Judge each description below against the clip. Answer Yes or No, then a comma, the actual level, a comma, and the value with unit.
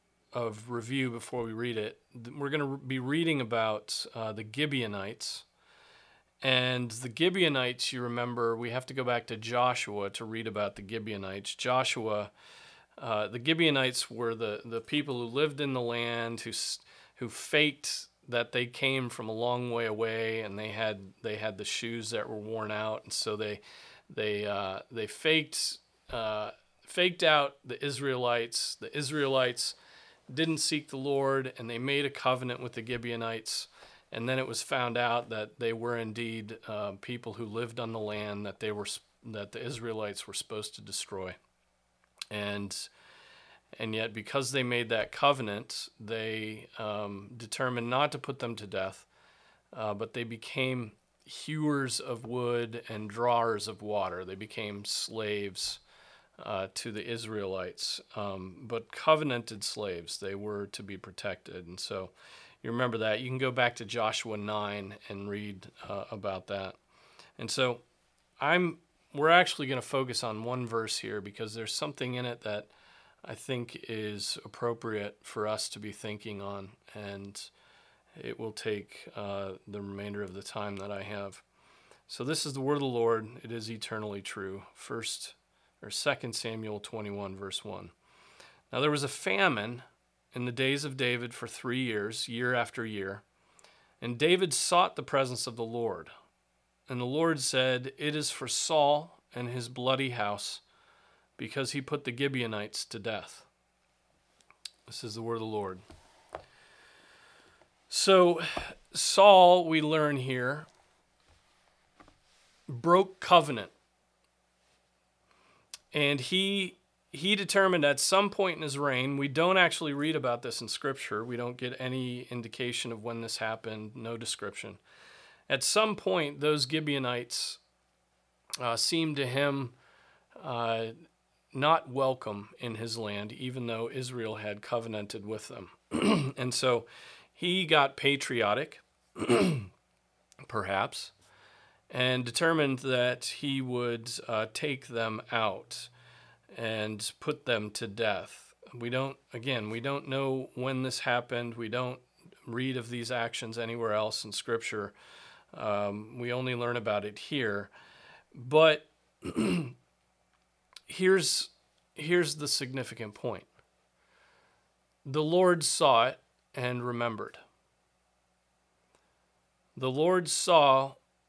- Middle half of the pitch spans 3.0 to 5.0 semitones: Yes, average, 3.9 semitones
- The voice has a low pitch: Yes, low, 120 Hz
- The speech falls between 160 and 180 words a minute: No, average, 145 wpm